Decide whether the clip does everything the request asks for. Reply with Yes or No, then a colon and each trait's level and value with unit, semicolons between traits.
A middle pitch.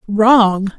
No: high, 215 Hz